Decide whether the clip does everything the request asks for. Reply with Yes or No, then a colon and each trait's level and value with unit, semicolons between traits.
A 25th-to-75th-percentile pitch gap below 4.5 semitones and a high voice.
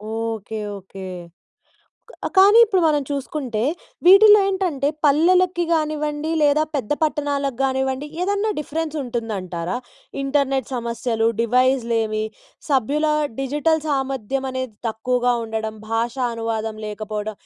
No: average, 5.0 semitones; very high, 265 Hz